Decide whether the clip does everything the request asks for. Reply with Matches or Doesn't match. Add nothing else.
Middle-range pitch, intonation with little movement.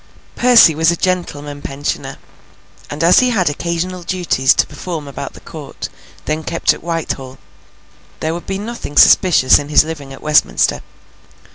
Doesn't match